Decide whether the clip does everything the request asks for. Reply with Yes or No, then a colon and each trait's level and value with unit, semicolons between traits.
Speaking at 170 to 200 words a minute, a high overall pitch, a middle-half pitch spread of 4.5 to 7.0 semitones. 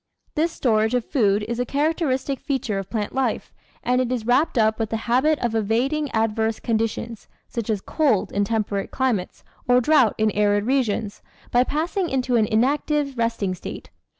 No: average, 175 wpm; high, 235 Hz; average, 3.7 semitones